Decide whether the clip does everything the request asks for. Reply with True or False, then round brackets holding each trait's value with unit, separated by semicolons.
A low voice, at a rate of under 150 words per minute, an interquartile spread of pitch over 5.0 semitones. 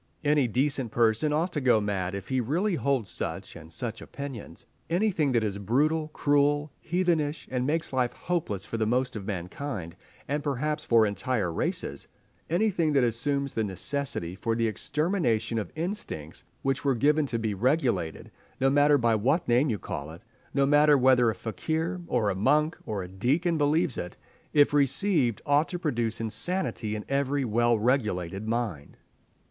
False (130 Hz; 160 wpm; 5.4 semitones)